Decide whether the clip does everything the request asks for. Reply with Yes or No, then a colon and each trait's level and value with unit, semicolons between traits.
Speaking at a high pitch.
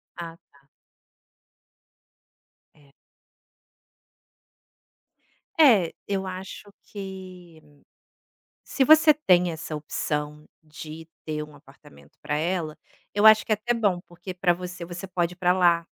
No: medium, 175 Hz